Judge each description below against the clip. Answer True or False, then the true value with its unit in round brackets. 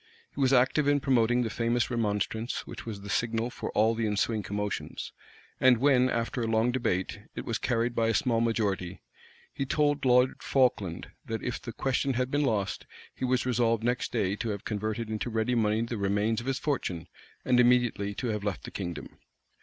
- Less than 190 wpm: False (195 wpm)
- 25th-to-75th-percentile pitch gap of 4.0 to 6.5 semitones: False (2.9 semitones)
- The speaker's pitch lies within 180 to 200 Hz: False (115 Hz)